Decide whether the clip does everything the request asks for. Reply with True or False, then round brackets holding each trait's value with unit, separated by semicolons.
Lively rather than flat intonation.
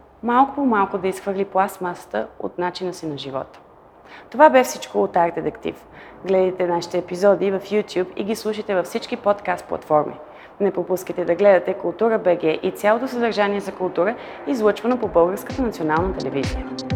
False (3.2 semitones)